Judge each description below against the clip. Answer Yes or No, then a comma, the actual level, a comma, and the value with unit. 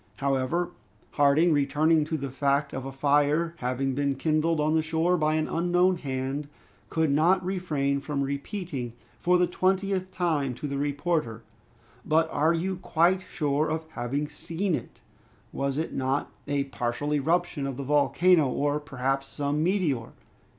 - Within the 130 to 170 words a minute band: Yes, average, 155 wpm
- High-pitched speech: No, medium, 150 Hz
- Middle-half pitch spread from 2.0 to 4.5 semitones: Yes, average, 3.3 semitones